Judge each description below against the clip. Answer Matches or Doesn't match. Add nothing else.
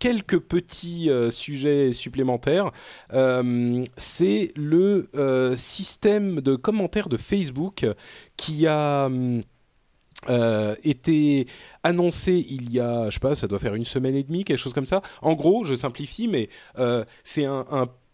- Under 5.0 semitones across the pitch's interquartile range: Doesn't match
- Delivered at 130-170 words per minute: Matches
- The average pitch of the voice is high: Doesn't match